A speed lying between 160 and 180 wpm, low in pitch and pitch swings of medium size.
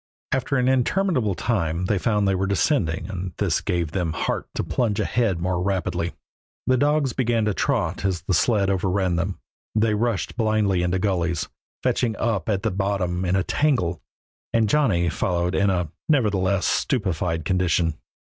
Yes: average, 165 wpm; very low, 95 Hz; average, 4.3 semitones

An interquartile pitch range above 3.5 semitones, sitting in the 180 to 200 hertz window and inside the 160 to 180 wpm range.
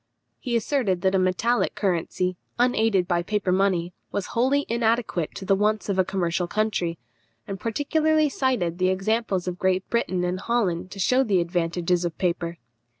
Yes: average, 4.4 semitones; high, 190 Hz; average, 170 wpm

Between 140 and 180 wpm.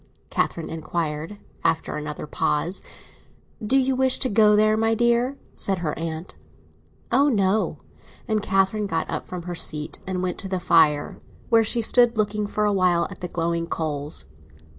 Yes: average, 160 wpm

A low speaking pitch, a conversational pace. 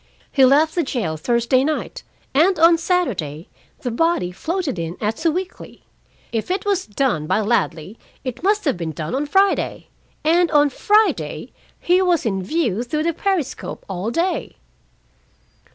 No: very high, 280 Hz; average, 150 wpm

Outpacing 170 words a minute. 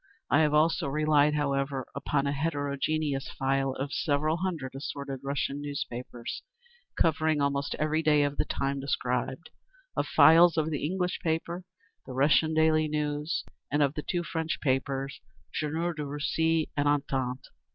No: average, 150 wpm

